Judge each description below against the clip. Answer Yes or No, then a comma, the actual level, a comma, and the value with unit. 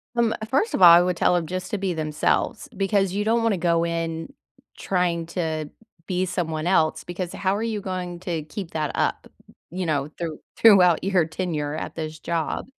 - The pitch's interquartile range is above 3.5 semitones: No, average, 2.9 semitones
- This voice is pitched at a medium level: Yes, medium, 175 Hz